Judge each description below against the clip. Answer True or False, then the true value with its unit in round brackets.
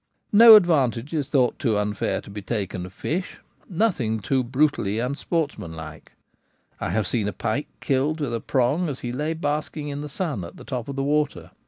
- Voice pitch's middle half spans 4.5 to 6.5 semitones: True (5.6 semitones)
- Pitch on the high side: False (135 Hz)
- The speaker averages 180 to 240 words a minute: True (190 wpm)